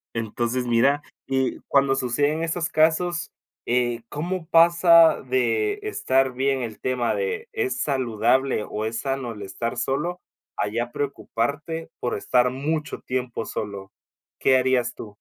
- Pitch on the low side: Yes, low, 130 Hz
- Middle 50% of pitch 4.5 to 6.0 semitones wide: Yes, average, 5.1 semitones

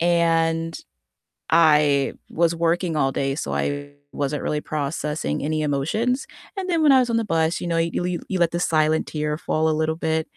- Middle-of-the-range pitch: Yes, medium, 160 Hz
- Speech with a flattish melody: Yes, narrow, 2.2 semitones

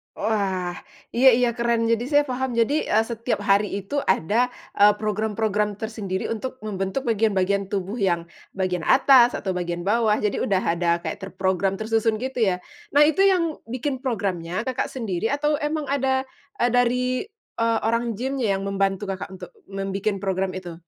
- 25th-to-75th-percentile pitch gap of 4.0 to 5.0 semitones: Yes, average, 4.3 semitones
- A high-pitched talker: Yes, high, 215 Hz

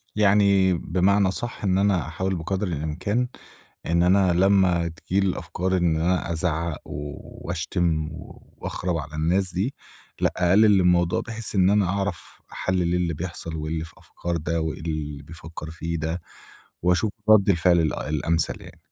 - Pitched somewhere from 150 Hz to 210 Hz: No, very low, 90 Hz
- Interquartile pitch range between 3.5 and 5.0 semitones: No, average, 2.8 semitones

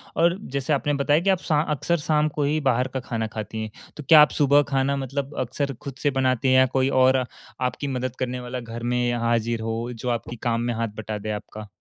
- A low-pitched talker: Yes, low, 130 Hz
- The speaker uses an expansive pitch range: No, average, 3.4 semitones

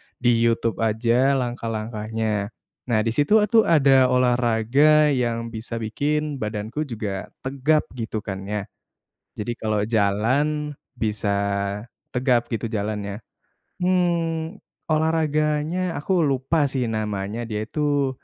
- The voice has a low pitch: Yes, low, 120 Hz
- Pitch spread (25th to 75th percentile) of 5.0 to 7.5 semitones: Yes, wide, 5.5 semitones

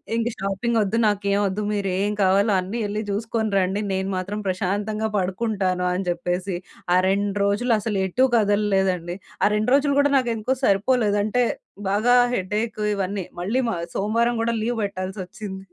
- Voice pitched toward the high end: Yes, high, 205 Hz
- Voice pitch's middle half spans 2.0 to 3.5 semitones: Yes, average, 2.7 semitones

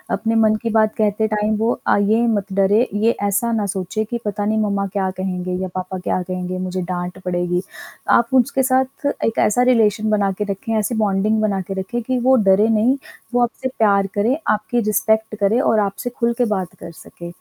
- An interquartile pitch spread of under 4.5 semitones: Yes, average, 2.8 semitones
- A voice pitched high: Yes, high, 210 Hz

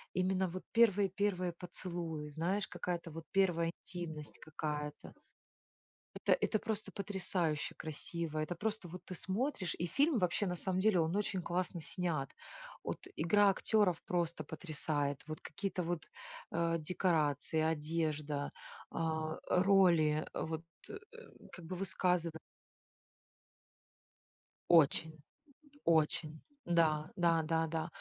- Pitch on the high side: No, medium, 170 Hz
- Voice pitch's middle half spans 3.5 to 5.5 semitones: No, average, 2.9 semitones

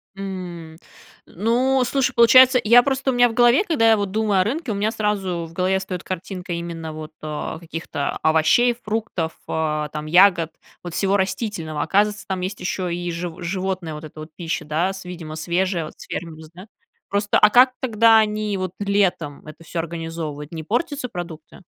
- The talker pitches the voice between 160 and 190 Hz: Yes, medium, 185 Hz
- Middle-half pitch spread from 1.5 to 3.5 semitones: No, average, 4.6 semitones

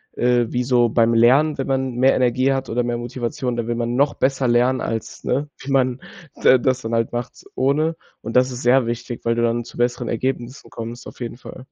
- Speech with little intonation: Yes, narrow, 1.7 semitones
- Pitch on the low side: Yes, low, 125 Hz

